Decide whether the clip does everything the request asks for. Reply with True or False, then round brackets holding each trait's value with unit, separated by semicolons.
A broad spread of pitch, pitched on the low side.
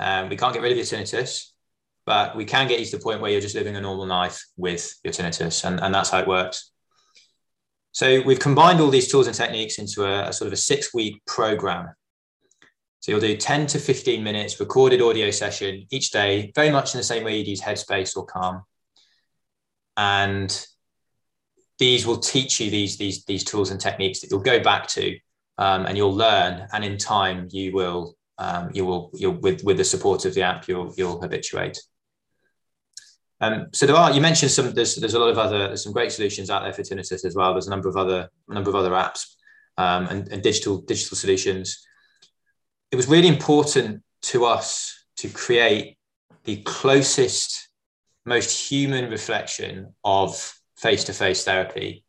True (6.9 semitones; 105 Hz)